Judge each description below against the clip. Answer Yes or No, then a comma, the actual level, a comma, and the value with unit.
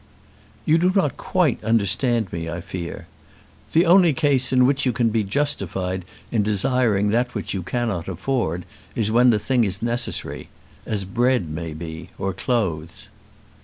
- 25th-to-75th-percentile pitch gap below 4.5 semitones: No, wide, 5.4 semitones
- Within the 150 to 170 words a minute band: Yes, average, 160 wpm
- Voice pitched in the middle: No, low, 110 Hz